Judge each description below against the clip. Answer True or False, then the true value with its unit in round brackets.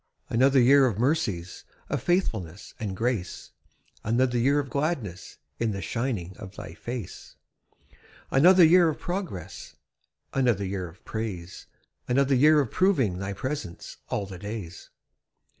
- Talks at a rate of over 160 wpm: False (135 wpm)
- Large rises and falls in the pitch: True (6.2 semitones)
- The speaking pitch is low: True (115 Hz)